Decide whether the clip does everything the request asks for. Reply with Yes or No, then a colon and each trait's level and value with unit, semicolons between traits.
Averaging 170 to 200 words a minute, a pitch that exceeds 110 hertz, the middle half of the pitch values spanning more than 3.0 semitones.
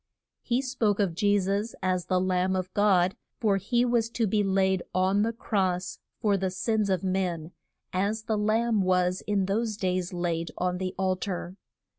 No: average, 180 wpm; high, 190 Hz; narrow, 2.6 semitones